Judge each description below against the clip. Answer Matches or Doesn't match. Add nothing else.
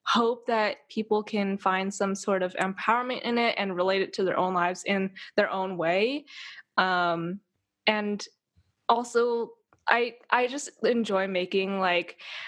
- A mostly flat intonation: Doesn't match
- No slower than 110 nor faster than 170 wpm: Matches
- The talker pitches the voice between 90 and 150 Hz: Doesn't match